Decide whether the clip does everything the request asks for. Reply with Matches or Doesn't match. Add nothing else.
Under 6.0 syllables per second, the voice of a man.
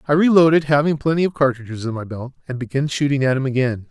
Doesn't match